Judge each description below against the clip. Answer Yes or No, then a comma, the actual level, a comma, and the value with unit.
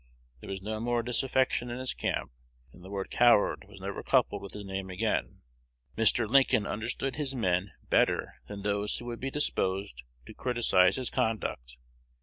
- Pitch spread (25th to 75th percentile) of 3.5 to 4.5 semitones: Yes, average, 4.0 semitones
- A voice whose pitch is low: Yes, low, 110 Hz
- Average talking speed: Yes, average, 170 wpm